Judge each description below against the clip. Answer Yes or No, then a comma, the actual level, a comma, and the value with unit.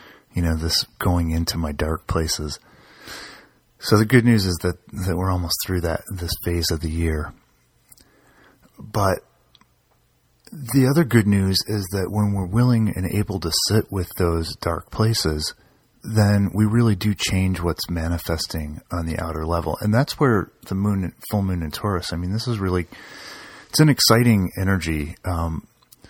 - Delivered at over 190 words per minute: No, average, 165 wpm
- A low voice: Yes, very low, 95 Hz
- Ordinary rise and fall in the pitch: Yes, average, 4.1 semitones